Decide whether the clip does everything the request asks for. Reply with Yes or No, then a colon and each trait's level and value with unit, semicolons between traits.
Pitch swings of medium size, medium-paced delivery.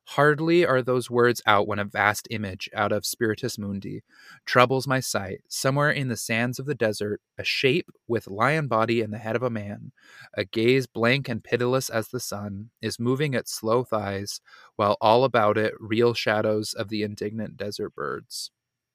Yes: average, 3.2 semitones; average, 185 wpm